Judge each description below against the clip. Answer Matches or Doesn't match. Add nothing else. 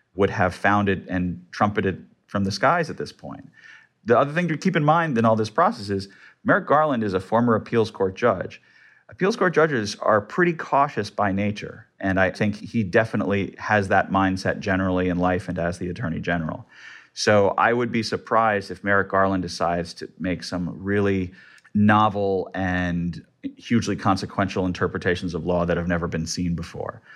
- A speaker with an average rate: Matches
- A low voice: Matches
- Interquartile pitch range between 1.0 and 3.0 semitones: Doesn't match